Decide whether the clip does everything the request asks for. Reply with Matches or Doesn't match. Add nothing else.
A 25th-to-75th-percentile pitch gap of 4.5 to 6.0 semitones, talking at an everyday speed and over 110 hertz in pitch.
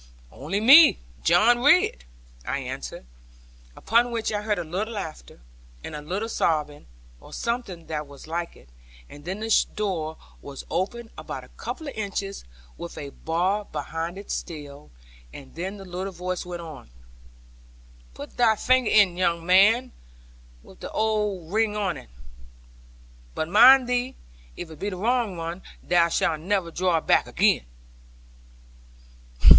Matches